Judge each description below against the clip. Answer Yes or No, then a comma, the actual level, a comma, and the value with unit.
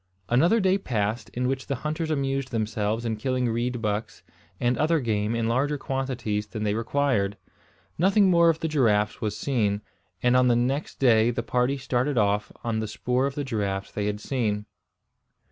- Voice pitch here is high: No, low, 120 Hz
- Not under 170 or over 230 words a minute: Yes, average, 180 wpm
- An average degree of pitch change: Yes, average, 4.2 semitones